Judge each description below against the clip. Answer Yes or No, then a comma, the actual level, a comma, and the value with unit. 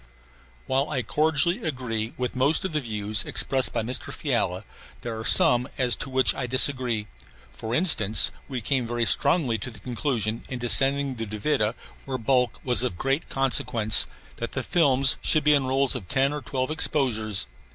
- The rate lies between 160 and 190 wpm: Yes, average, 175 wpm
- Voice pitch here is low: Yes, low, 130 Hz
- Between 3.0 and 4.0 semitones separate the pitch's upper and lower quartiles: Yes, average, 3.4 semitones